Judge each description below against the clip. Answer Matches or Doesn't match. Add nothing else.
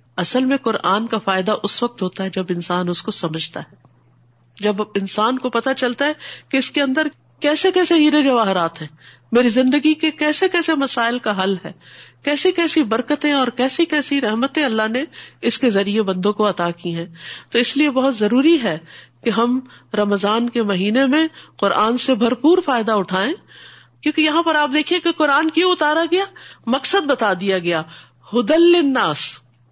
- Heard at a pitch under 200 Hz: Doesn't match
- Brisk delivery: Doesn't match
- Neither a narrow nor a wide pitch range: Doesn't match